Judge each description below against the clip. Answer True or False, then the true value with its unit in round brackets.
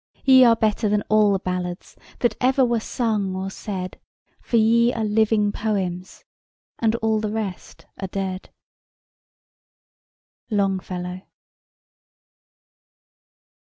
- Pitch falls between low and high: False (210 Hz)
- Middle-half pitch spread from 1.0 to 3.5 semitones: True (2.8 semitones)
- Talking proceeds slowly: True (110 wpm)